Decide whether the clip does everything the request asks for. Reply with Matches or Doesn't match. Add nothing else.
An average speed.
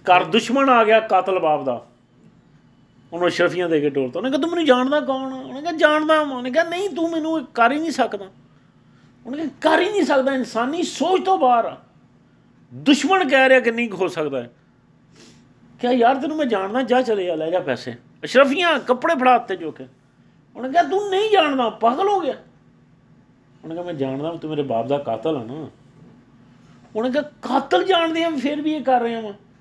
Matches